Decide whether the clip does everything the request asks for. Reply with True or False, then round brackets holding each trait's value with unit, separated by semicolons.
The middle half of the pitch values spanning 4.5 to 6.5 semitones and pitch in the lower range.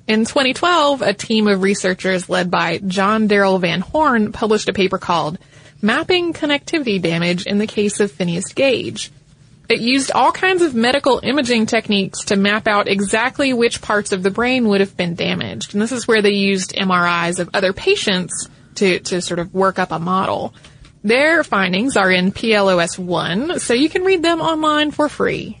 False (5.1 semitones; 205 Hz)